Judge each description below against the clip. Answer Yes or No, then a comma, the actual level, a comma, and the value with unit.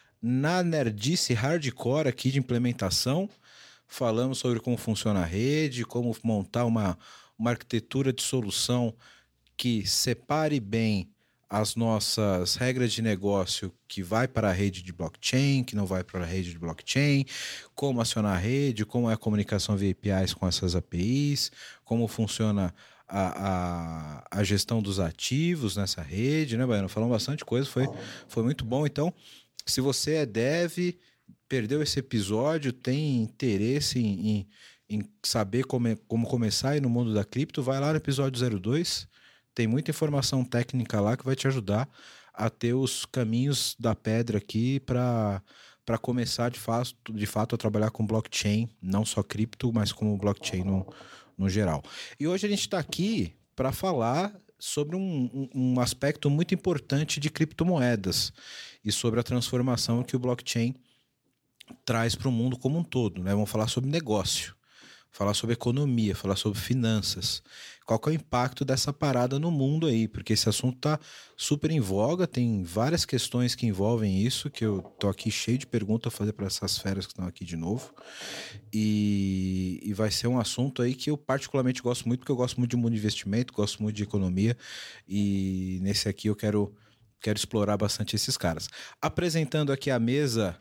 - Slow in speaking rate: No, average, 170 wpm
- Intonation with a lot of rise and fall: No, average, 4.2 semitones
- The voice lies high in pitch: No, low, 115 Hz